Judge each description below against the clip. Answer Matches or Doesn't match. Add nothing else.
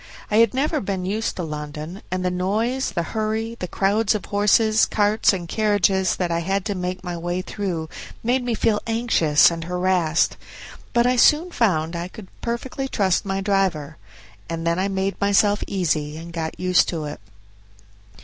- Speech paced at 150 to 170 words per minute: Doesn't match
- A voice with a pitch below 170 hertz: Doesn't match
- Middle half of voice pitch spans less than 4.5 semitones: Matches